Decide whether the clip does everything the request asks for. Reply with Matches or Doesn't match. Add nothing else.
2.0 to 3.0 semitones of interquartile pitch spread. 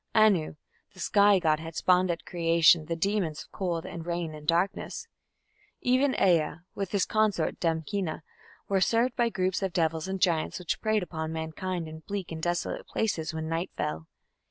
Doesn't match